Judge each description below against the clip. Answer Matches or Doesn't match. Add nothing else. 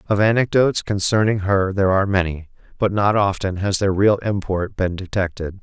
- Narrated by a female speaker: Doesn't match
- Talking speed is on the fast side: Doesn't match